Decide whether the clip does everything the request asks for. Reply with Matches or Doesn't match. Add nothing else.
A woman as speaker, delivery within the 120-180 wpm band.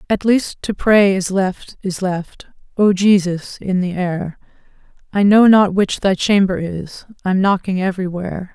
Matches